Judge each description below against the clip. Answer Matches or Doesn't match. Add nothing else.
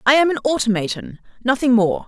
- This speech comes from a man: Doesn't match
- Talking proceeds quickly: Doesn't match